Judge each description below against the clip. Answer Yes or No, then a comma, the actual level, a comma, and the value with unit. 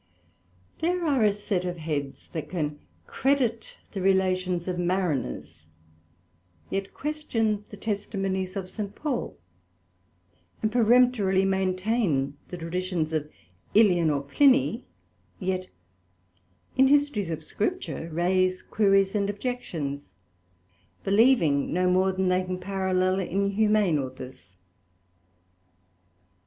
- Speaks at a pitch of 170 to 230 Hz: Yes, high, 190 Hz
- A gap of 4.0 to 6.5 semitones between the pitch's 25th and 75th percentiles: No, average, 3.5 semitones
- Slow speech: Yes, slow, 110 wpm